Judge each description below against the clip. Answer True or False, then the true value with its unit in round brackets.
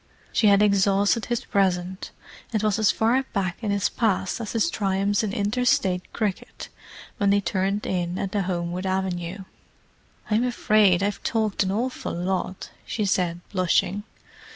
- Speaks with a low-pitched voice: False (200 Hz)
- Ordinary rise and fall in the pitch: False (2.3 semitones)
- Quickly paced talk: False (155 wpm)